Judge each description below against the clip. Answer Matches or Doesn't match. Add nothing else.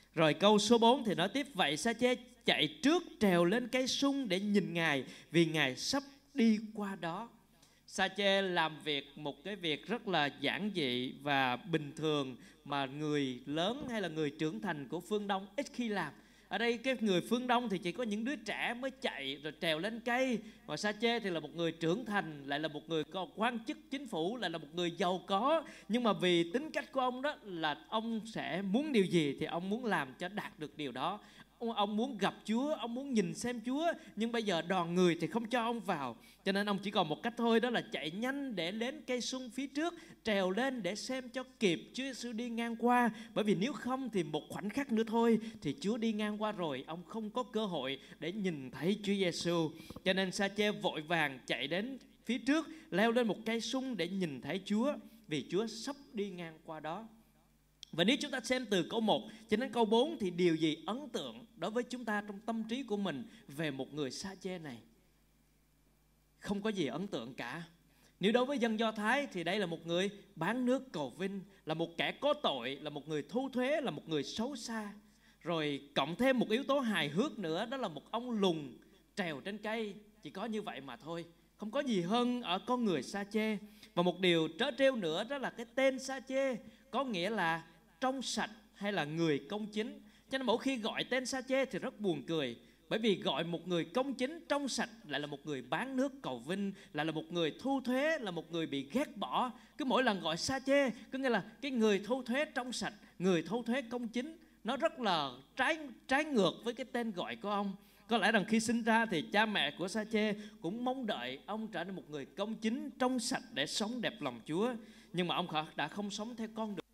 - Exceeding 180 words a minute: Matches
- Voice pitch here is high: Matches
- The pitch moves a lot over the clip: Matches